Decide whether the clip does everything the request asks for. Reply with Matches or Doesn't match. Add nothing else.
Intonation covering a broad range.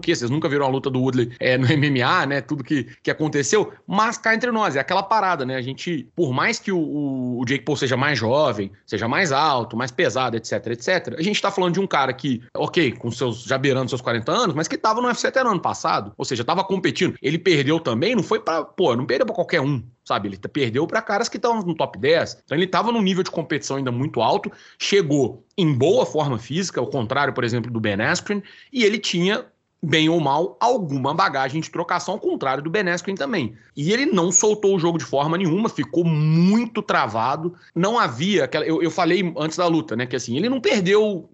Matches